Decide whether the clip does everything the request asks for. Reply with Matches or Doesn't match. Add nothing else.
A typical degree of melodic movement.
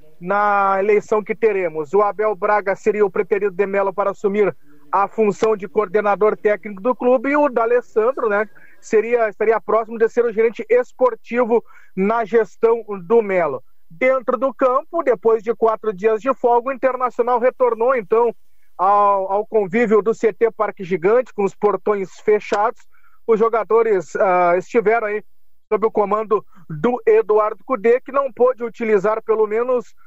Matches